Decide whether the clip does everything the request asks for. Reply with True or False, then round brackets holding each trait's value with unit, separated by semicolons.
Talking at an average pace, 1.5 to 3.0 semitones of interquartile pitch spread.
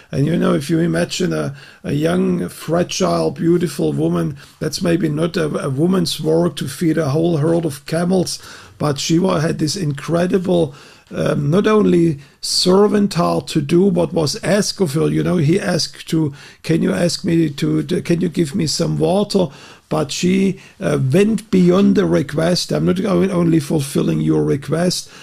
True (170 wpm; 2.5 semitones)